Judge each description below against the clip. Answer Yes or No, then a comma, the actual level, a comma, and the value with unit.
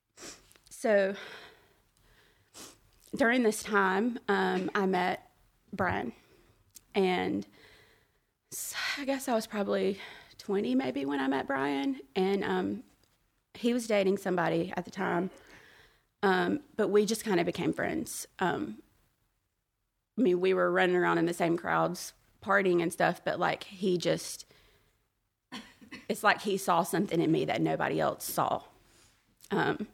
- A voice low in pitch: No, high, 190 Hz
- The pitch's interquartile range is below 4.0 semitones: Yes, average, 3.2 semitones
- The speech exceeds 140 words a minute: No, slow, 135 wpm